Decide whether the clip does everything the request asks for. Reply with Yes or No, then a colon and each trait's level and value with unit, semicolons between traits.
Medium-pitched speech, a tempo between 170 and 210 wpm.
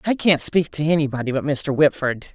Yes: medium, 145 Hz; fast, 205 wpm